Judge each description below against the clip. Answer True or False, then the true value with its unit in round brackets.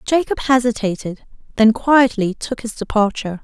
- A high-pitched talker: True (230 Hz)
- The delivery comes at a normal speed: False (120 wpm)